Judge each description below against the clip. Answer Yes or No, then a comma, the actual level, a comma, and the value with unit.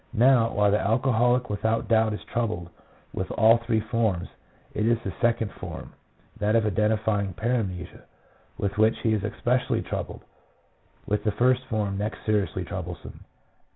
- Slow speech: No, average, 155 wpm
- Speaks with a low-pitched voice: Yes, low, 110 Hz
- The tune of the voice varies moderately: No, narrow, 2.3 semitones